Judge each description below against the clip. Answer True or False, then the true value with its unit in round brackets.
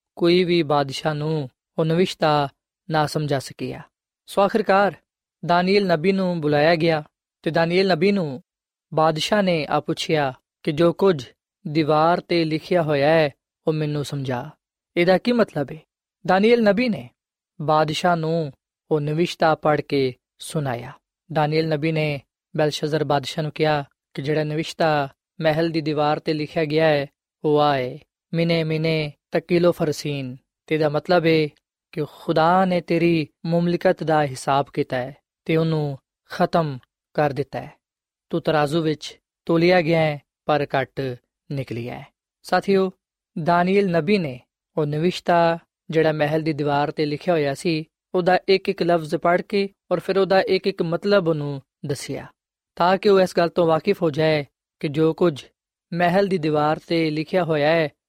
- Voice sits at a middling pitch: True (160 Hz)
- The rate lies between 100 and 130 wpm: False (145 wpm)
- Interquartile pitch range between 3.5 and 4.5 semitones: False (2.8 semitones)